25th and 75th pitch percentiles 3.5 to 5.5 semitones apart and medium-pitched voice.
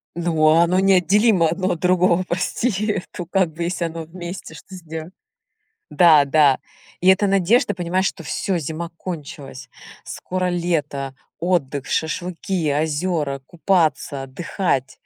No: average, 3.0 semitones; medium, 170 Hz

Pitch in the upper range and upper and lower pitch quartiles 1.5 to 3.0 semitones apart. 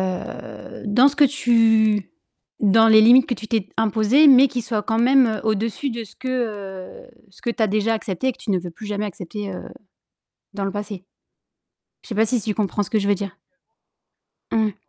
Yes: high, 220 Hz; narrow, 2.5 semitones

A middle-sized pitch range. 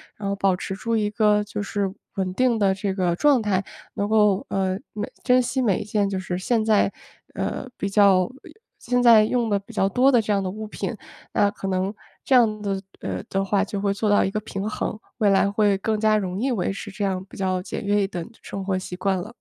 No: narrow, 1.9 semitones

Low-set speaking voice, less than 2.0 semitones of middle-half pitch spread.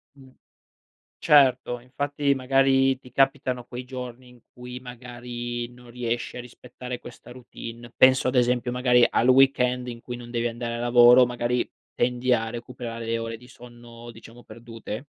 Yes: low, 125 Hz; narrow, 1.1 semitones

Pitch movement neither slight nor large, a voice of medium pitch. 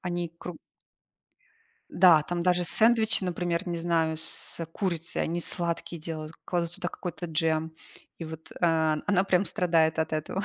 No: narrow, 1.9 semitones; medium, 170 Hz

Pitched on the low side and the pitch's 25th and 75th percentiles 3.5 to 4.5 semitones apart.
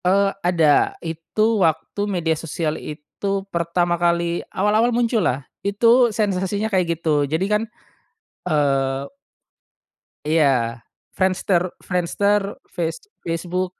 No: medium, 175 Hz; average, 3.9 semitones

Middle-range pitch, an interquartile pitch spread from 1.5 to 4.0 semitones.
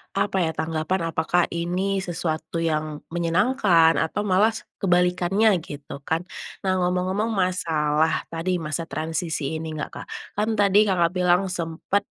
Yes: medium, 175 Hz; average, 2.8 semitones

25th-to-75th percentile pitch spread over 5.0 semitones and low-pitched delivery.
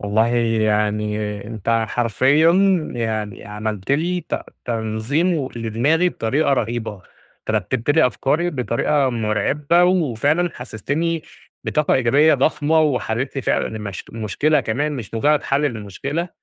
Yes: wide, 5.5 semitones; low, 125 Hz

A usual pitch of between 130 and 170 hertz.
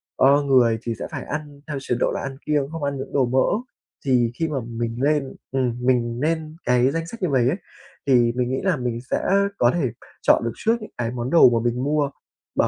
Yes: low, 135 Hz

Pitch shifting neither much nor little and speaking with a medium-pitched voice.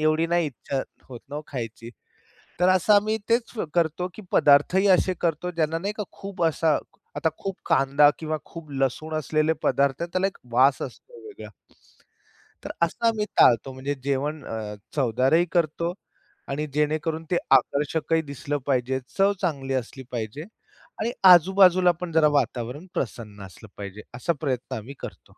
Yes: average, 4.6 semitones; medium, 150 Hz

